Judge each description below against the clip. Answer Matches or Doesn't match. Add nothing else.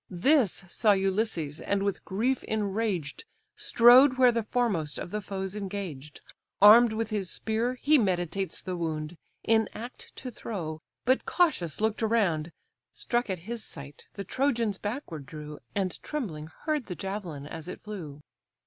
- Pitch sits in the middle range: Doesn't match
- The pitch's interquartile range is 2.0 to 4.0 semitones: Doesn't match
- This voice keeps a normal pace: Matches